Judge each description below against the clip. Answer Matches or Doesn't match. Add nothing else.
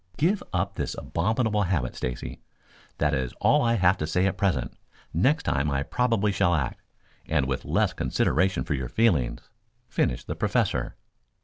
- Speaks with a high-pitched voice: Doesn't match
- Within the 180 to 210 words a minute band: Doesn't match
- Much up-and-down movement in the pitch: Matches